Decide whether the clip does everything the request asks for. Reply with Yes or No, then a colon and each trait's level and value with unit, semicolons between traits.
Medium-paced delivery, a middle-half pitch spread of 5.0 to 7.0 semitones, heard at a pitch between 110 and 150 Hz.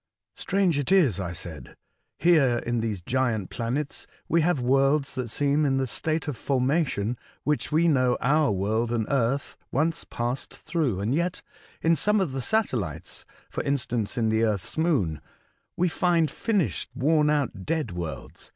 Yes: average, 170 wpm; wide, 5.6 semitones; low, 135 Hz